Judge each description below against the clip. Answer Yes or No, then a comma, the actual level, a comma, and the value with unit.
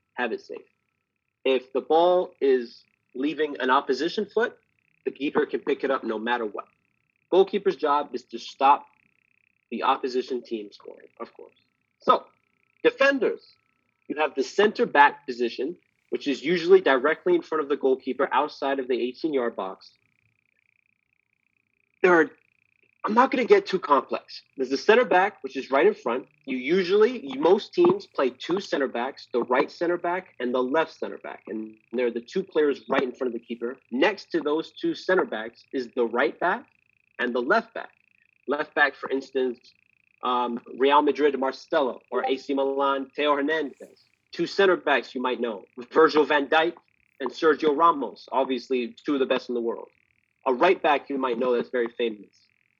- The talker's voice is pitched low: No, medium, 150 Hz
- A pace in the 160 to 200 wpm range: Yes, average, 180 wpm